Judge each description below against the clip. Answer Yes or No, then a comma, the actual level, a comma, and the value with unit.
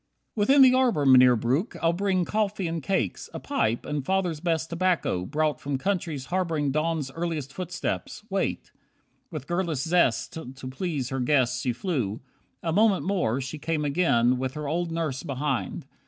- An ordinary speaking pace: Yes, average, 170 wpm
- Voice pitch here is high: No, medium, 155 Hz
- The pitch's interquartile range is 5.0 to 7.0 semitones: Yes, average, 5.3 semitones